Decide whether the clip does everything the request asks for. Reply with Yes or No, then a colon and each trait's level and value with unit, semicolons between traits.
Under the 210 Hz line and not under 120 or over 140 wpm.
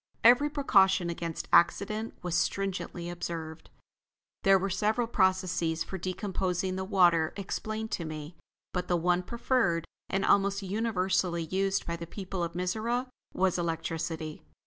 Yes: medium, 185 Hz; slow, 135 wpm